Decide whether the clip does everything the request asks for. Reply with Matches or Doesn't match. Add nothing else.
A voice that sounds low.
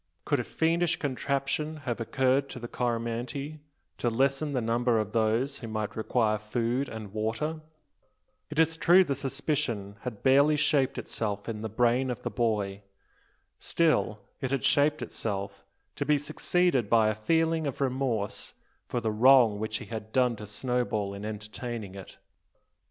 Matches